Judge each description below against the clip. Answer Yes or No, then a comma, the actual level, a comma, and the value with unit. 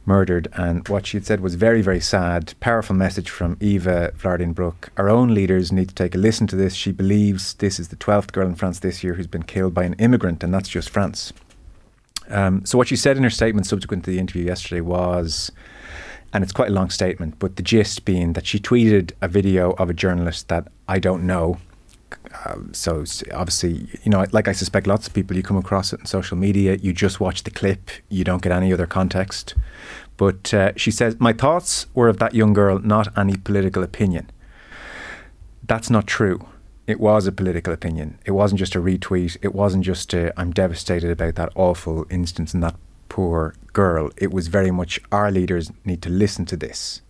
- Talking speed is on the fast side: Yes, fast, 210 wpm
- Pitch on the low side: Yes, very low, 95 Hz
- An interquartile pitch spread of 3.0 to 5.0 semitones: No, narrow, 2.4 semitones